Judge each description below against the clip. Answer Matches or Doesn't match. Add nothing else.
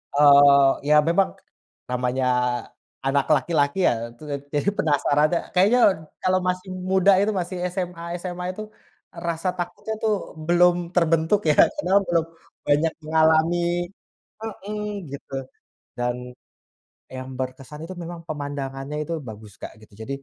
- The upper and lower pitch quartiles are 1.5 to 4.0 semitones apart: Doesn't match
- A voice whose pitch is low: Doesn't match